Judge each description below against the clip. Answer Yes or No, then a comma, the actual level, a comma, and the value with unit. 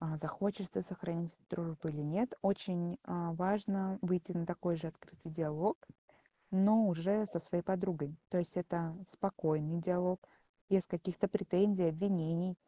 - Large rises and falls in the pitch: No, average, 2.7 semitones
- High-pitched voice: No, medium, 180 Hz